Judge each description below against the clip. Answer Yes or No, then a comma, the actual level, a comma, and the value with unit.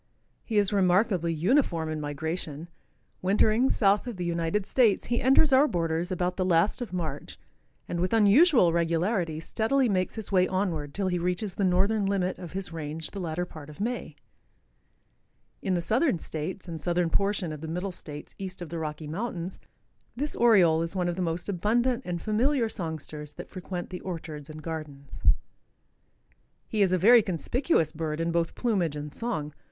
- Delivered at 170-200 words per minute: Yes, average, 180 wpm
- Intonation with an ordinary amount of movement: Yes, average, 4.1 semitones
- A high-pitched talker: No, medium, 180 Hz